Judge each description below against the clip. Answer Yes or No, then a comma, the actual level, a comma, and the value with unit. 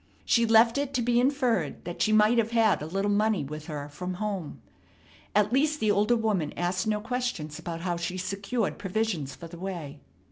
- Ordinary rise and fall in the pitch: Yes, average, 4.9 semitones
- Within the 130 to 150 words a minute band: No, average, 200 wpm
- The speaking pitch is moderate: No, high, 205 Hz